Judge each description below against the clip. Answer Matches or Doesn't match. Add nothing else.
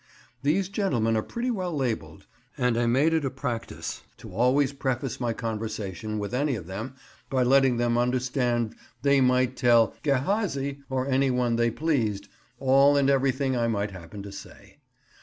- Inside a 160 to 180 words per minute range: Matches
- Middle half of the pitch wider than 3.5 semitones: Doesn't match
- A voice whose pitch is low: Matches